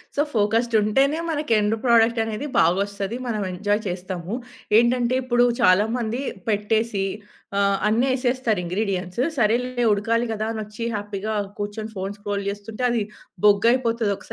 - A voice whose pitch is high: Yes, high, 215 Hz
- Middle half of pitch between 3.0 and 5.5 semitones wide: No, narrow, 2.6 semitones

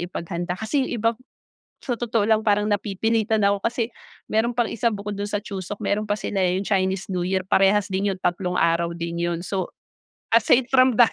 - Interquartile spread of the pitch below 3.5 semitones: Yes, average, 3.1 semitones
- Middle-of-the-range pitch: No, high, 205 Hz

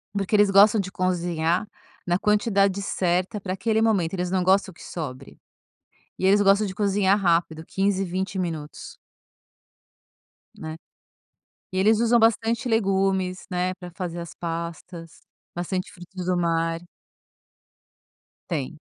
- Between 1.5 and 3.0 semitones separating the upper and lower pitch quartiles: Yes, narrow, 2.6 semitones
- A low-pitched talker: No, medium, 185 Hz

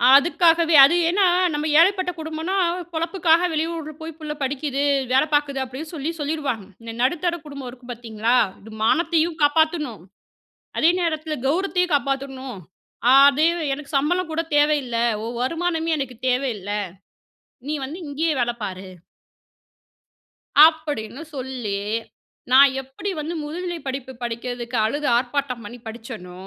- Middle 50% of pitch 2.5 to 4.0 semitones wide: No, average, 4.4 semitones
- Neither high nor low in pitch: No, very high, 290 Hz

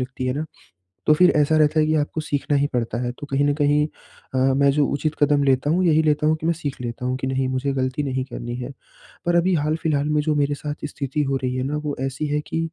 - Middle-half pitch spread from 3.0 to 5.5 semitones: No, narrow, 2.5 semitones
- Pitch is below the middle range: No, medium, 145 Hz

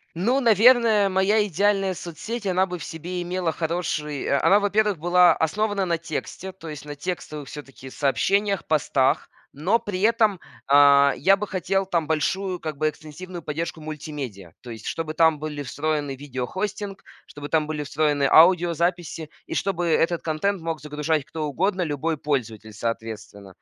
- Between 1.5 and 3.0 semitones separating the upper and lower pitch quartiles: No, average, 4.5 semitones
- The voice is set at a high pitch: No, medium, 165 Hz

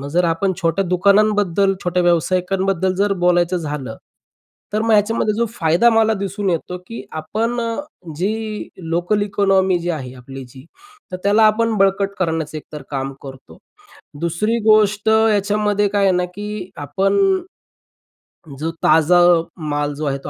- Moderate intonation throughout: Yes, average, 4.0 semitones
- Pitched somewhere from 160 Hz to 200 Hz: Yes, high, 190 Hz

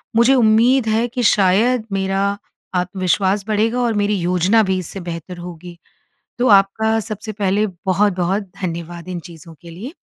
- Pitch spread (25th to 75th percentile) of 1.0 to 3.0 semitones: No, average, 3.5 semitones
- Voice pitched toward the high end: Yes, high, 195 Hz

